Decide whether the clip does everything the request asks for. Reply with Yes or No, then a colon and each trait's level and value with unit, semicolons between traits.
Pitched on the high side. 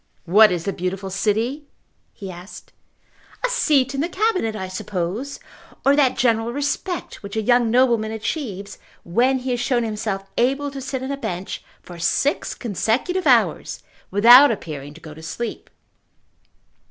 Yes: high, 230 Hz